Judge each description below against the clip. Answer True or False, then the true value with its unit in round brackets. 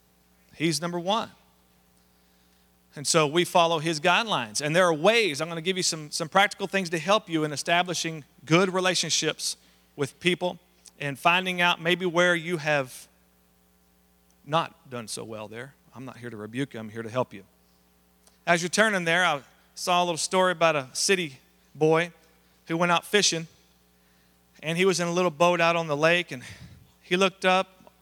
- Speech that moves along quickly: False (185 wpm)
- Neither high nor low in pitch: True (160 Hz)